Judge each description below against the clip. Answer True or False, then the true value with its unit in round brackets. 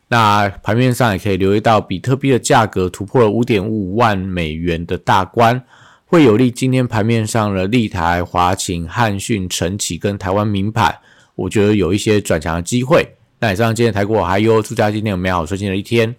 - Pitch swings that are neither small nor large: True (3.6 semitones)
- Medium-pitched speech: False (105 Hz)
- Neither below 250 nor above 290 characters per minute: False (310 characters per minute)